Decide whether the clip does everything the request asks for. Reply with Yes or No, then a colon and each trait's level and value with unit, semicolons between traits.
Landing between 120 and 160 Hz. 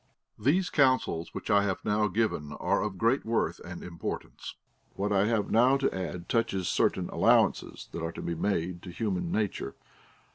No: low, 100 Hz